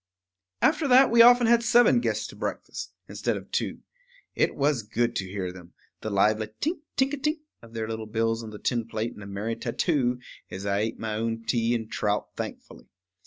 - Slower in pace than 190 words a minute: No, fast, 205 wpm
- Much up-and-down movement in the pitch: Yes, wide, 8.2 semitones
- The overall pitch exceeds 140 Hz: No, low, 115 Hz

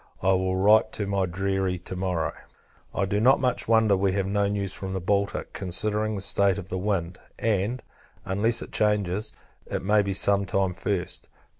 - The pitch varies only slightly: Yes, narrow, 1.9 semitones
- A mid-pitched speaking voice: No, low, 100 Hz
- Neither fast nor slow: Yes, average, 185 wpm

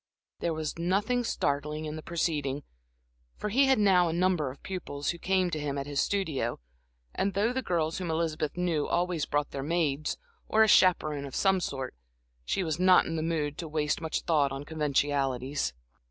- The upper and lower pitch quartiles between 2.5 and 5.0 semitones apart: Yes, average, 3.9 semitones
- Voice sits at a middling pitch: Yes, medium, 160 Hz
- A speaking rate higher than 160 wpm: Yes, average, 190 wpm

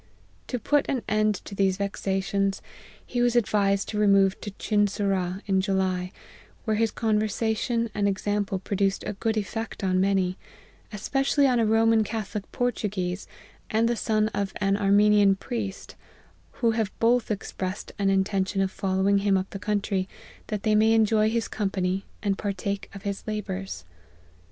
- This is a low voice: No, high, 205 Hz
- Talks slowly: No, average, 160 wpm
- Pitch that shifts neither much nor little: No, narrow, 2.1 semitones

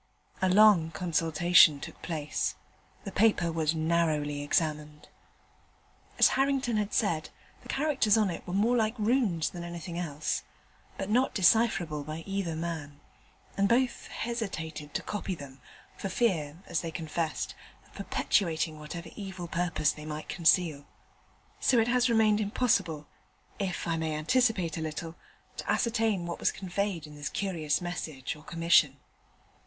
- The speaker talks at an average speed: Yes, average, 145 wpm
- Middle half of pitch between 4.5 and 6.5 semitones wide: Yes, average, 4.9 semitones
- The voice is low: No, medium, 170 Hz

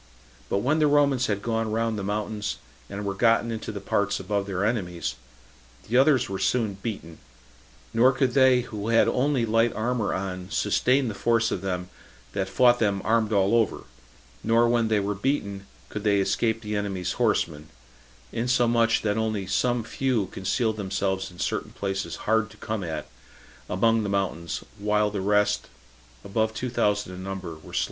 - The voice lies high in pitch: No, low, 105 Hz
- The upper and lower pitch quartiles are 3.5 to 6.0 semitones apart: No, average, 3.0 semitones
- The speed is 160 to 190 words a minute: Yes, average, 175 wpm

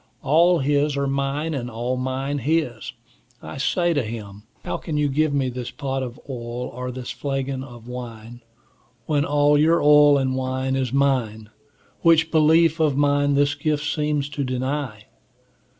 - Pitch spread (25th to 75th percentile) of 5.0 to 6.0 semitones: No, average, 2.7 semitones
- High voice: No, medium, 140 Hz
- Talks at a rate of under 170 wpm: Yes, average, 160 wpm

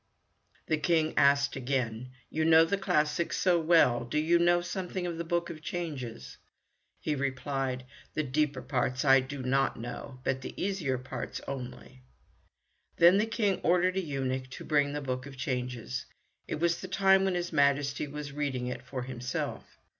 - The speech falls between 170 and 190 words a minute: Yes, average, 175 wpm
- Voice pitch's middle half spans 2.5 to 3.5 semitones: No, average, 4.8 semitones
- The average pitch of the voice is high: No, medium, 145 Hz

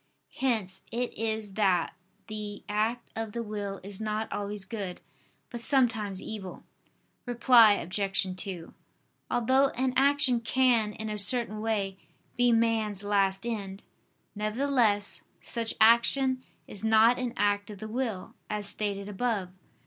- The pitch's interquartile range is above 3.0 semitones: No, average, 2.7 semitones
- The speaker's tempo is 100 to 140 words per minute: Yes, slow, 135 wpm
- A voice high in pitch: Yes, high, 215 Hz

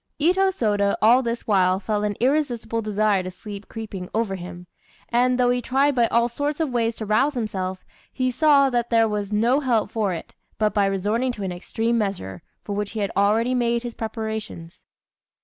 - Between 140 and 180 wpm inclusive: No, average, 195 wpm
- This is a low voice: No, high, 225 Hz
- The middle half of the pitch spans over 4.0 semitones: No, average, 3.4 semitones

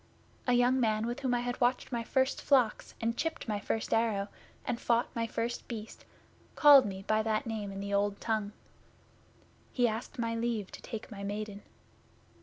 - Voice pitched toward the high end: Yes, high, 230 Hz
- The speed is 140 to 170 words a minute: No, average, 185 wpm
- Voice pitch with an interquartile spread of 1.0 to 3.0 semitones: Yes, narrow, 2.4 semitones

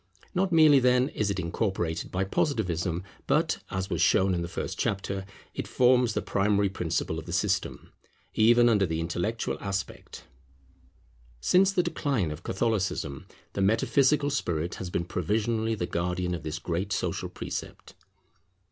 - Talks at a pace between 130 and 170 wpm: Yes, average, 150 wpm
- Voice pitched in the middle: No, low, 100 Hz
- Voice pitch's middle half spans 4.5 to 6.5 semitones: Yes, average, 5.2 semitones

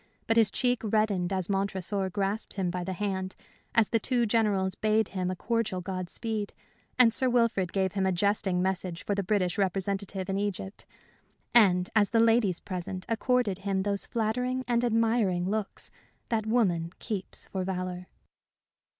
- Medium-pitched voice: No, high, 200 Hz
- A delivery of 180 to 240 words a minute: No, average, 160 wpm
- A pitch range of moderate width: Yes, average, 3.1 semitones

